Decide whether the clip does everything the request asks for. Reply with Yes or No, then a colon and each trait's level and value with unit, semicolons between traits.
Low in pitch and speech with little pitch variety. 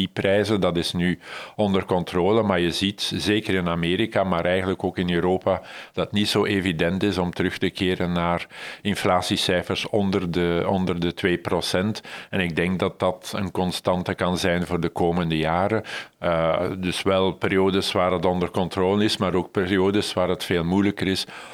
Yes: very low, 95 Hz; narrow, 1.8 semitones